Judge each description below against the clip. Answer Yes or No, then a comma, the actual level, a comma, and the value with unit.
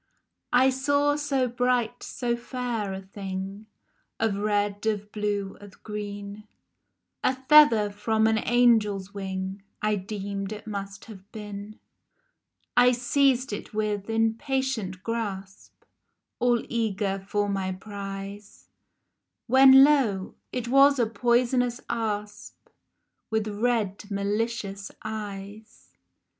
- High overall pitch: Yes, high, 215 Hz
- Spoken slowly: Yes, slow, 110 wpm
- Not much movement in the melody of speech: No, average, 3.2 semitones